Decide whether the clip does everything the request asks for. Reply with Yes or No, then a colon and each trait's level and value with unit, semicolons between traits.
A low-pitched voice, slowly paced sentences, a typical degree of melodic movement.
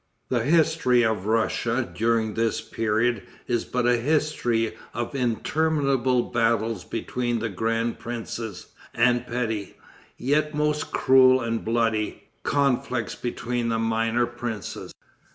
No: low, 120 Hz; slow, 115 wpm; narrow, 1.9 semitones